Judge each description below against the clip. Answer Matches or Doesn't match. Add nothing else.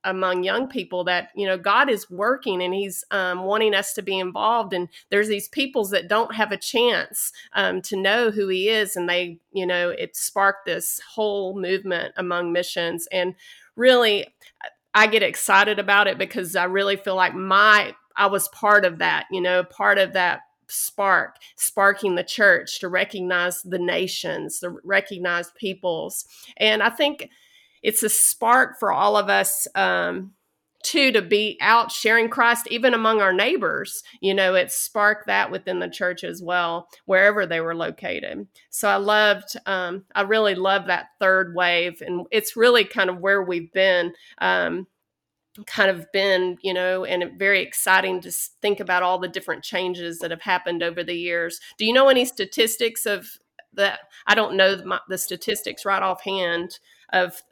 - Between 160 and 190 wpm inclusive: Matches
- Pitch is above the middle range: Matches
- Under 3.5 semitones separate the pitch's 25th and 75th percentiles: Matches